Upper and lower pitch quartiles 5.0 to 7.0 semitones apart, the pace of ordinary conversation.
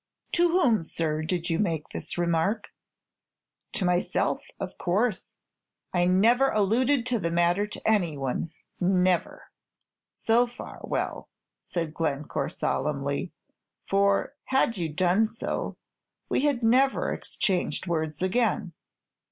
No: wide, 5.4 semitones; slow, 120 wpm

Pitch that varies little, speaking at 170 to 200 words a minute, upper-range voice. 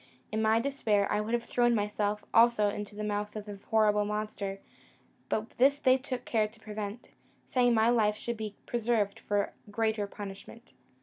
Yes: narrow, 2.1 semitones; average, 175 wpm; high, 215 Hz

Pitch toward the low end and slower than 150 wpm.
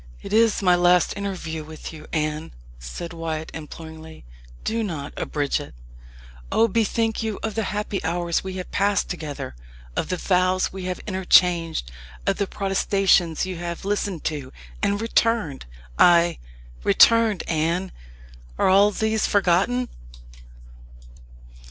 No: medium, 180 Hz; slow, 135 wpm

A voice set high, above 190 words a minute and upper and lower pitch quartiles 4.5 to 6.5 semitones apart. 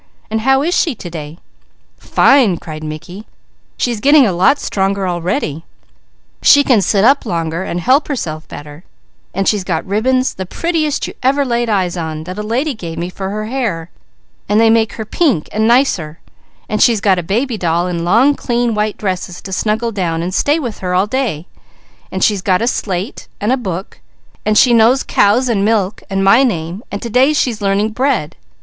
Yes: high, 210 Hz; average, 200 wpm; average, 5.3 semitones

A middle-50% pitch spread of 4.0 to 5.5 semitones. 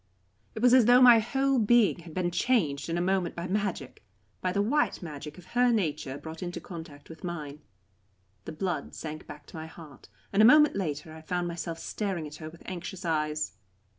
Yes: average, 4.8 semitones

